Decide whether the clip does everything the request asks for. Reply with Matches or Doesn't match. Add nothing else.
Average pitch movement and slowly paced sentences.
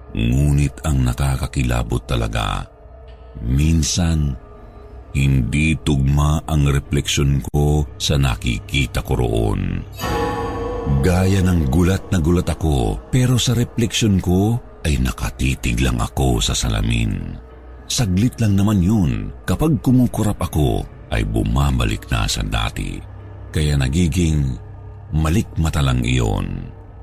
Doesn't match